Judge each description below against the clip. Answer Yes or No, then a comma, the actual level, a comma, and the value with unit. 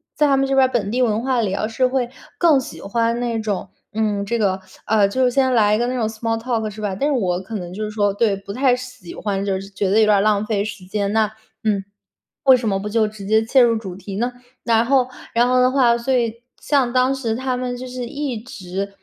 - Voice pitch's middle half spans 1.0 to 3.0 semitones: No, average, 3.6 semitones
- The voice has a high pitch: Yes, high, 225 Hz